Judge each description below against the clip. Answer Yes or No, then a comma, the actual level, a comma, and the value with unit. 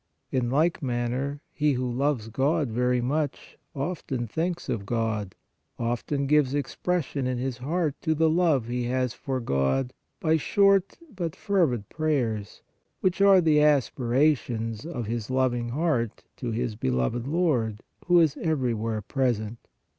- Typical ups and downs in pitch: Yes, average, 4.7 semitones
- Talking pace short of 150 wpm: Yes, average, 140 wpm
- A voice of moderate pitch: No, low, 130 Hz